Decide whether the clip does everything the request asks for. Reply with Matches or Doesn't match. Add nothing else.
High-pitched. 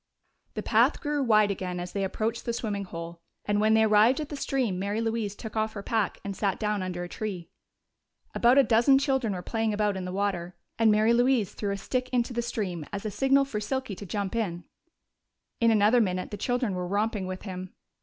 Matches